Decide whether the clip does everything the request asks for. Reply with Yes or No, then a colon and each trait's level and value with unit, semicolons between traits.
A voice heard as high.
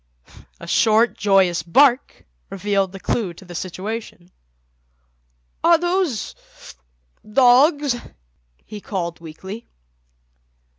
Yes: high, 200 Hz